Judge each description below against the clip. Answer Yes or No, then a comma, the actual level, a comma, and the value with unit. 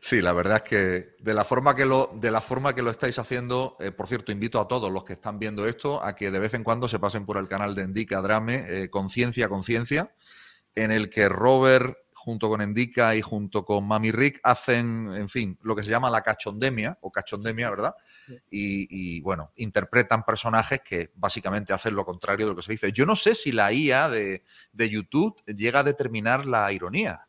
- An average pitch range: Yes, average, 3.4 semitones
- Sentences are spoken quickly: Yes, fast, 210 wpm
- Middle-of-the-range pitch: No, low, 110 Hz